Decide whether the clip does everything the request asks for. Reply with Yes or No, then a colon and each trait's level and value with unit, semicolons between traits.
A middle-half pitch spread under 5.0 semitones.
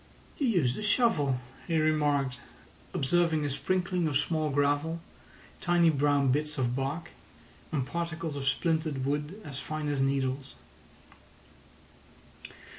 Yes: average, 3.3 semitones